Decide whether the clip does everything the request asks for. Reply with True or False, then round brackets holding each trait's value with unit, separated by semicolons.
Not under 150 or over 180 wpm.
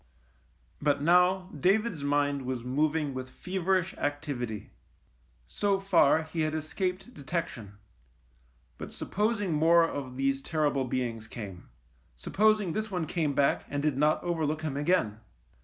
False (140 wpm)